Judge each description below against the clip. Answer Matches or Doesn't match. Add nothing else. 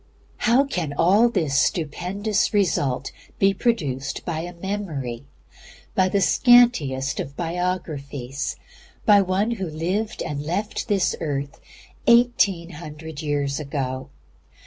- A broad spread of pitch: Matches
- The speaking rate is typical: Doesn't match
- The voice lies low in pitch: Doesn't match